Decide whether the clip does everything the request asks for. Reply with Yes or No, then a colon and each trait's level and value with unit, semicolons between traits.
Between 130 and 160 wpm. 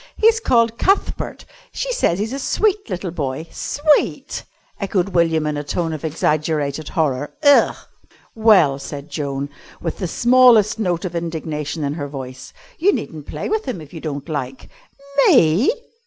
Yes: average, 155 wpm